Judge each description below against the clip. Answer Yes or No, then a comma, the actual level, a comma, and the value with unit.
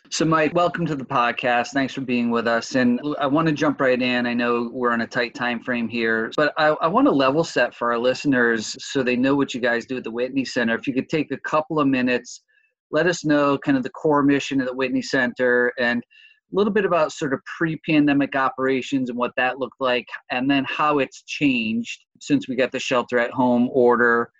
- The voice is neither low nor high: No, low, 130 Hz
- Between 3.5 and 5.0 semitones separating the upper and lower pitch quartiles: Yes, average, 3.8 semitones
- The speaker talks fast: Yes, fast, 235 wpm